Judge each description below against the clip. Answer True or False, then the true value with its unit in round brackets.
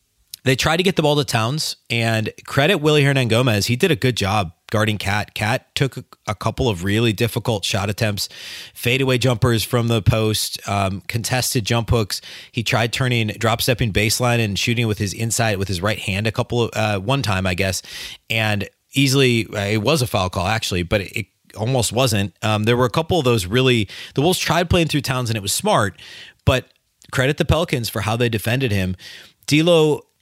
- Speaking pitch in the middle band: False (115 Hz)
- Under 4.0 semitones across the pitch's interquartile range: True (3.4 semitones)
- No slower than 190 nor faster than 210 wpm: True (205 wpm)